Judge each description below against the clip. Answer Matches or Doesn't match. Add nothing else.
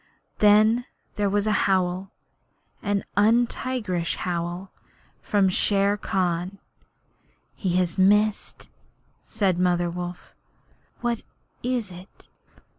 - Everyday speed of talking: Doesn't match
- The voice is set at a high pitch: Matches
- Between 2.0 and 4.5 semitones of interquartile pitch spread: Matches